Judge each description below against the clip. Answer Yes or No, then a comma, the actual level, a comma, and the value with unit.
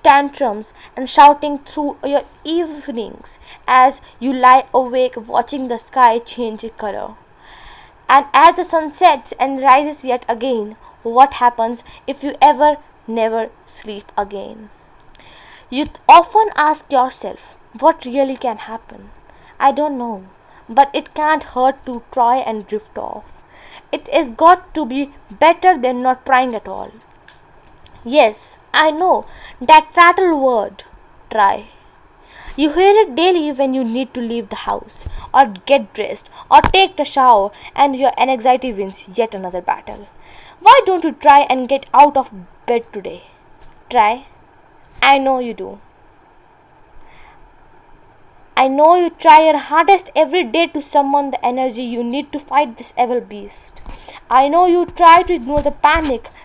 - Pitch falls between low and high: No, very high, 275 Hz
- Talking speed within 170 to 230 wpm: No, average, 145 wpm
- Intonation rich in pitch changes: No, average, 4.2 semitones